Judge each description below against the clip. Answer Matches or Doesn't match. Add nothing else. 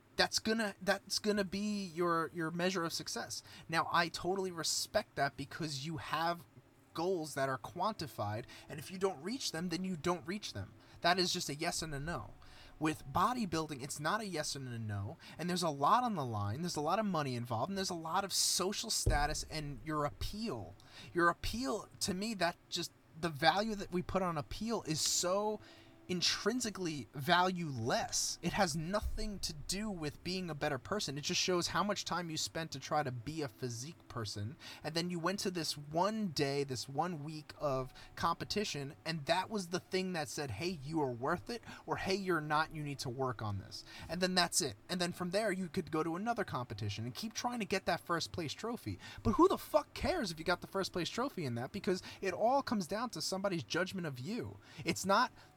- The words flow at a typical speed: Doesn't match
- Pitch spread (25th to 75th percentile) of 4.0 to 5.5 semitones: Matches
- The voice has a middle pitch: Matches